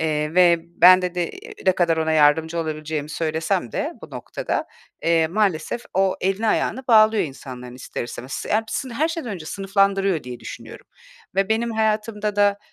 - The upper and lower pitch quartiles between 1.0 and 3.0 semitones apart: No, average, 4.9 semitones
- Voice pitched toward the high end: No, medium, 180 Hz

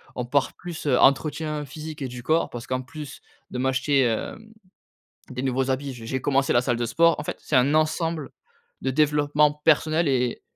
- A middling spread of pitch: Yes, average, 3.0 semitones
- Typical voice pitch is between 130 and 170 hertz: Yes, medium, 140 Hz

